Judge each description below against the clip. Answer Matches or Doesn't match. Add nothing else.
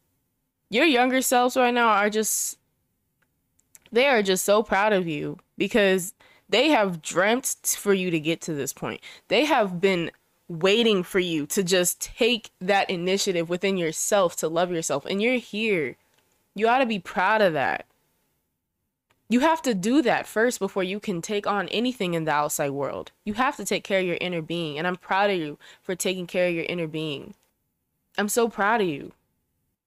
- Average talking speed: Matches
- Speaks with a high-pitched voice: Matches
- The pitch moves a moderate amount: Matches